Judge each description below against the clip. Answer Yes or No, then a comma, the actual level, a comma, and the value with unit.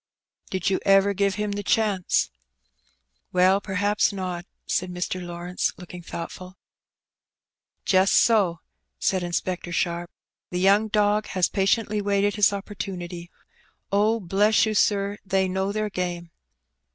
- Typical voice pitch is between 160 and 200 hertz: Yes, high, 190 Hz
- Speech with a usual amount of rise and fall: No, narrow, 2.3 semitones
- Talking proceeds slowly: Yes, slow, 130 wpm